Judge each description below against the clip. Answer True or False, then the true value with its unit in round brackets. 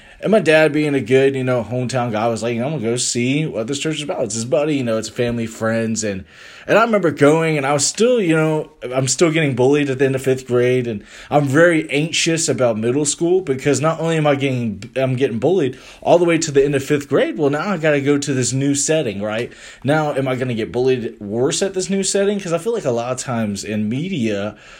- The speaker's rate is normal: False (255 wpm)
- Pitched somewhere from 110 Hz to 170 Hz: True (135 Hz)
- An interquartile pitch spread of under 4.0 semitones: False (4.6 semitones)